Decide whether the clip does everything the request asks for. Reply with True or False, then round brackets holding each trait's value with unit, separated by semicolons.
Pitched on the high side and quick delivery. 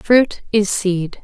False (205 Hz; 145 wpm)